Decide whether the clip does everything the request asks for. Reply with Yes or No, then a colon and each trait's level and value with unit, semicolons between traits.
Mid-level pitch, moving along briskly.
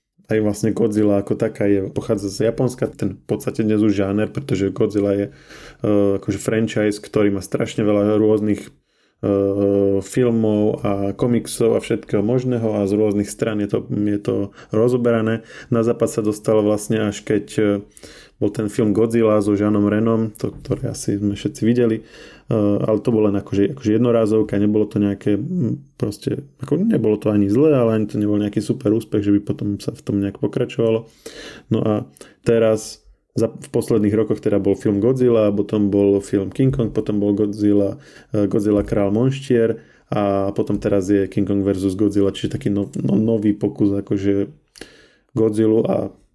No: low, 105 Hz; fast, 175 wpm